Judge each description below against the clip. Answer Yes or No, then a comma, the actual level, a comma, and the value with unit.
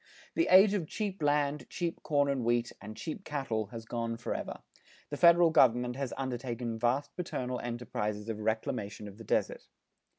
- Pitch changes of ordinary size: Yes, average, 4.5 semitones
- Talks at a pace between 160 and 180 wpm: Yes, average, 165 wpm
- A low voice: Yes, low, 125 Hz